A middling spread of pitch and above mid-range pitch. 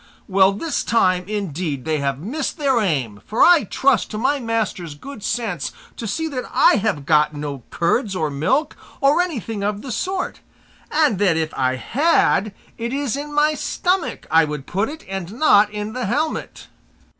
No: wide, 8.9 semitones; high, 210 Hz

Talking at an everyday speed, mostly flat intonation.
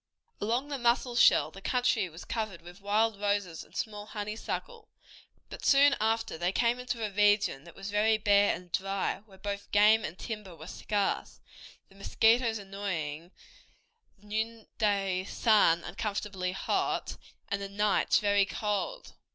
Yes: average, 145 wpm; narrow, 2.3 semitones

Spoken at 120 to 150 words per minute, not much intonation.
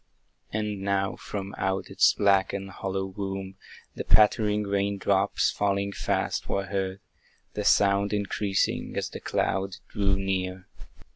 Yes: slow, 135 wpm; narrow, 0.8 semitones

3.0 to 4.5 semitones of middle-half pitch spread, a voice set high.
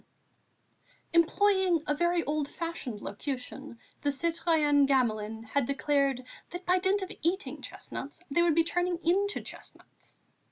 Yes: average, 4.2 semitones; very high, 315 Hz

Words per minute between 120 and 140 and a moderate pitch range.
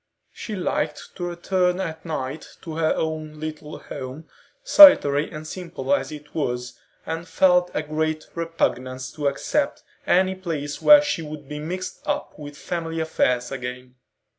No: average, 150 wpm; average, 3.2 semitones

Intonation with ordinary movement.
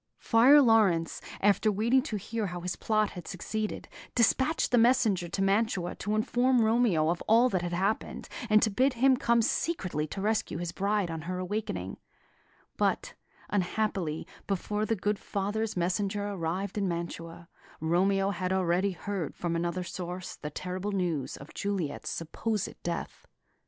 Yes: average, 3.7 semitones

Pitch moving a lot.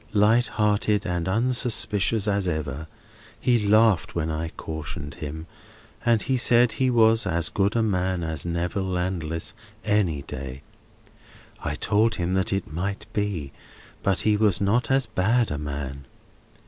No: average, 5.0 semitones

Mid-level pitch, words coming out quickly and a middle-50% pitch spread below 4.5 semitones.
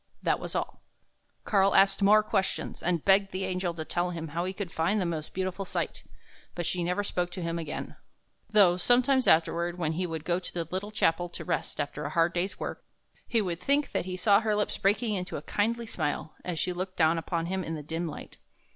Yes: medium, 180 Hz; fast, 225 wpm; average, 2.9 semitones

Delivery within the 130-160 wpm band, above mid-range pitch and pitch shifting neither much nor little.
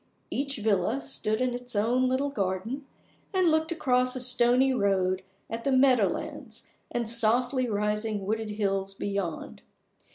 Yes: average, 140 wpm; high, 235 Hz; average, 3.8 semitones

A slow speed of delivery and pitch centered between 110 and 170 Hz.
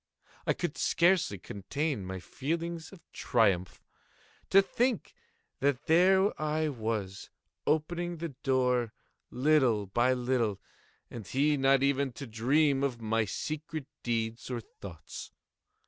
Yes: slow, 120 wpm; low, 135 Hz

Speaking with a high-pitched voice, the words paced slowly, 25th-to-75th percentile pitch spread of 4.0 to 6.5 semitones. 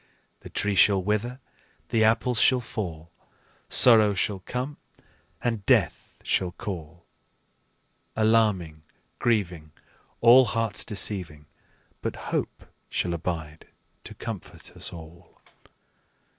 No: low, 100 Hz; slow, 105 wpm; average, 4.9 semitones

